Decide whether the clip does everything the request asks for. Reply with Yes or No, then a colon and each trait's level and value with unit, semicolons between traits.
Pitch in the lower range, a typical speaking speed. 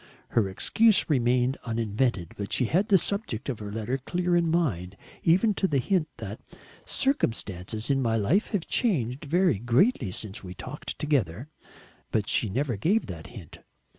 Yes: low, 125 Hz; average, 165 wpm